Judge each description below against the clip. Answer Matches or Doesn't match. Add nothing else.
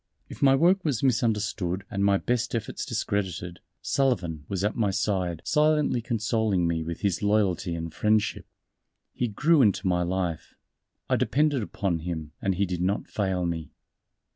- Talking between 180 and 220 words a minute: Doesn't match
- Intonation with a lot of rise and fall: Doesn't match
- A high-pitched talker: Doesn't match